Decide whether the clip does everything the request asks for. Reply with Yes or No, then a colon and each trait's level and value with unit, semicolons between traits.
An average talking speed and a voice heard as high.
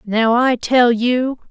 Yes: average, 160 wpm; high, 240 Hz